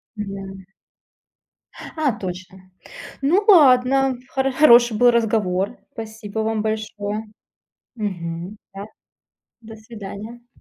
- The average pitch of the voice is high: Yes, high, 220 Hz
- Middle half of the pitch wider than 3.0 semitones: Yes, average, 3.4 semitones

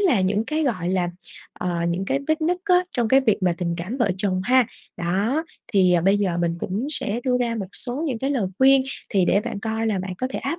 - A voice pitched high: Yes, high, 220 Hz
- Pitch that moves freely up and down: Yes, wide, 6.1 semitones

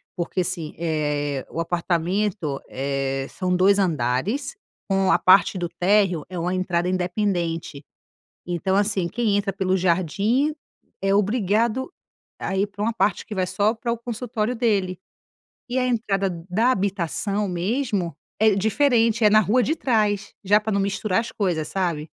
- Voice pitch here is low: No, high, 195 Hz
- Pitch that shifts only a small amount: No, average, 3.6 semitones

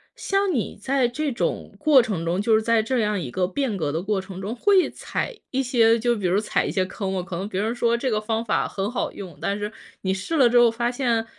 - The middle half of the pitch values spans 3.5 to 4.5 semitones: Yes, average, 4.2 semitones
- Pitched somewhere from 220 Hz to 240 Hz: Yes, high, 225 Hz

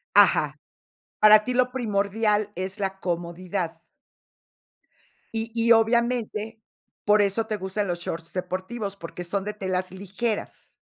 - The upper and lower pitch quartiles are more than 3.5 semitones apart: No, average, 3.2 semitones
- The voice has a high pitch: Yes, high, 200 Hz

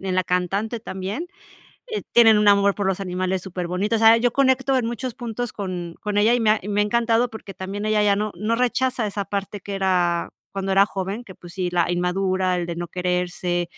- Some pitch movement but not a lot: Yes, average, 3.5 semitones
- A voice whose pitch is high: Yes, high, 200 Hz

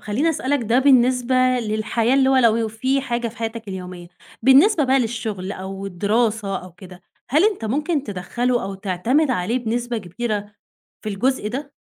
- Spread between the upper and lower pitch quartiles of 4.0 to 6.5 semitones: Yes, average, 4.3 semitones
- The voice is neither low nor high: No, high, 230 Hz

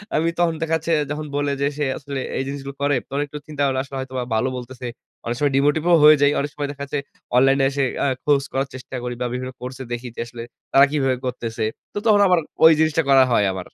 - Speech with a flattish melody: Yes, narrow, 2.2 semitones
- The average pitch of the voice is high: No, medium, 140 Hz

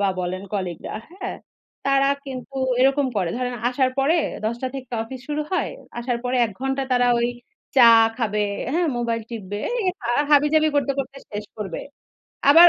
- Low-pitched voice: No, very high, 255 Hz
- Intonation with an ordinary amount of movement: Yes, average, 3.8 semitones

